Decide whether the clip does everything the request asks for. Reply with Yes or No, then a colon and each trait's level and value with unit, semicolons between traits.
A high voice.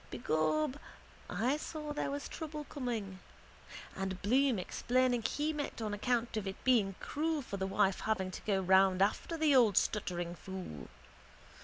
Yes: high, 220 Hz